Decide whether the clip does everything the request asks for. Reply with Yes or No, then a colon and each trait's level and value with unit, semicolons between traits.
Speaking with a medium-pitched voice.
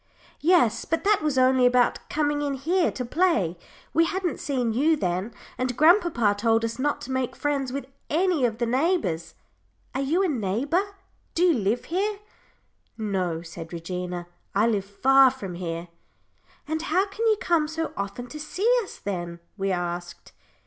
No: very high, 260 Hz